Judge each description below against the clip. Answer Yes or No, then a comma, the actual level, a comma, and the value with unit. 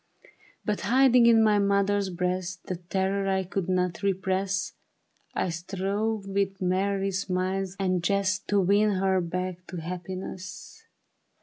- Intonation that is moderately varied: No, narrow, 1.5 semitones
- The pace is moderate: No, slow, 130 wpm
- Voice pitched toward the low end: No, high, 190 Hz